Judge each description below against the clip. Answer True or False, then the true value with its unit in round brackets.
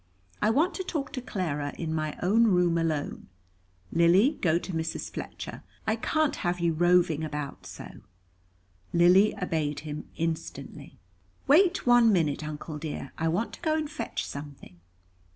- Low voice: False (170 Hz)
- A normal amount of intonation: False (6.2 semitones)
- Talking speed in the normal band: True (150 wpm)